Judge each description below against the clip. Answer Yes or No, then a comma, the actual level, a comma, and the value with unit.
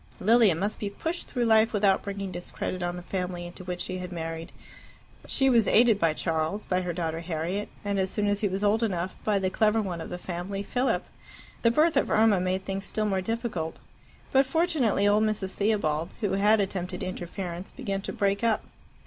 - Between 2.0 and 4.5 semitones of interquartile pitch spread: Yes, average, 3.3 semitones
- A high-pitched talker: Yes, high, 195 Hz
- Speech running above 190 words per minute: Yes, average, 200 wpm